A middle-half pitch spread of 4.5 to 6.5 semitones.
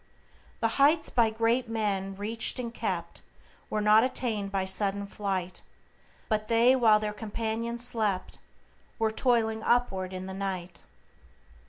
No: average, 2.8 semitones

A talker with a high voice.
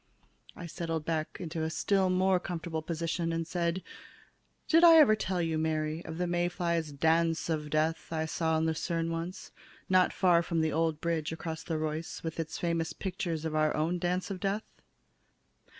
No: medium, 165 Hz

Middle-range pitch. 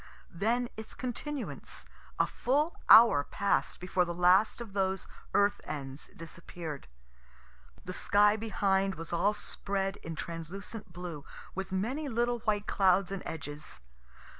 No: high, 195 Hz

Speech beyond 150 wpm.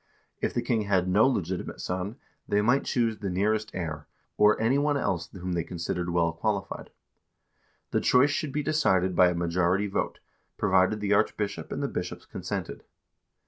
Yes: average, 170 wpm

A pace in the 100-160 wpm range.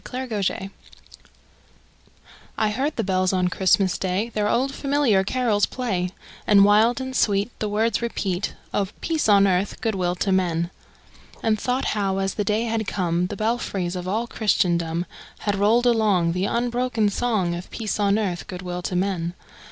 No: average, 170 wpm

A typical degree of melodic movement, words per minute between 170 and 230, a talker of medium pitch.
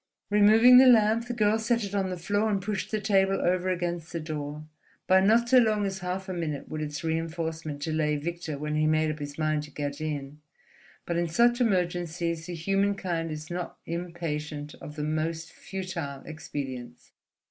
Yes: average, 4.2 semitones; average, 190 wpm; medium, 170 Hz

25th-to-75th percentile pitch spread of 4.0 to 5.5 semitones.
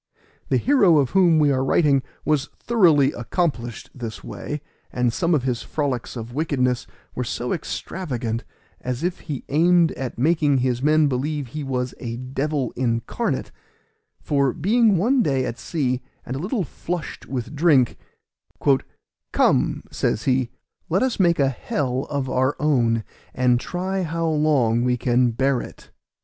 Yes: average, 4.4 semitones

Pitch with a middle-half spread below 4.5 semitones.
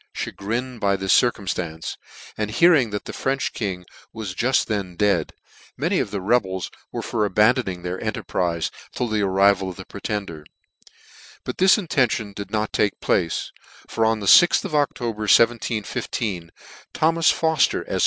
Yes: average, 4.0 semitones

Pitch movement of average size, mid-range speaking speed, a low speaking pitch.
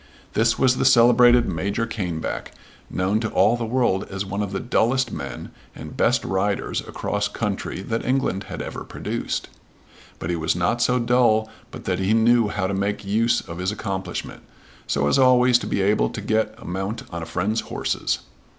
Yes: average, 3.8 semitones; average, 185 wpm; low, 105 Hz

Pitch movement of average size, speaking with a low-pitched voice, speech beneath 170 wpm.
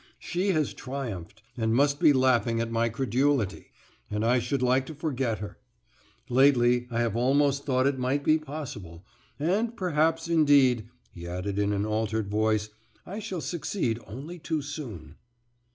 Yes: average, 4.8 semitones; low, 130 Hz; average, 155 wpm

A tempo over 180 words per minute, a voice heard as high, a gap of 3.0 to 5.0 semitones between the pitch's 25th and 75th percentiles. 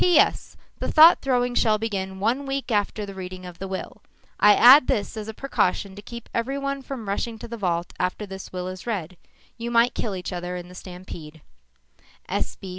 Yes: average, 190 wpm; high, 205 Hz; average, 4.5 semitones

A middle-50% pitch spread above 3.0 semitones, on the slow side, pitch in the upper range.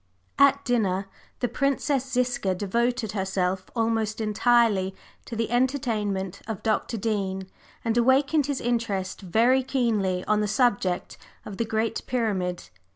Yes: average, 4.1 semitones; slow, 130 wpm; high, 225 Hz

